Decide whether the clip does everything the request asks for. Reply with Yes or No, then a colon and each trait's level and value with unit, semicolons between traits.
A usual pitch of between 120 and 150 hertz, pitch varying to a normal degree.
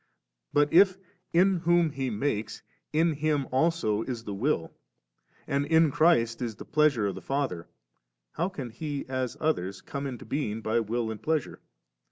No: medium, 140 Hz; wide, 5.7 semitones